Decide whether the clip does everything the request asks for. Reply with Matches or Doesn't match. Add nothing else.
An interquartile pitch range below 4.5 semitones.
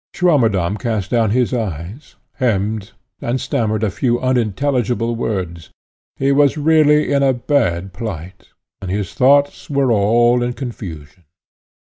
Doesn't match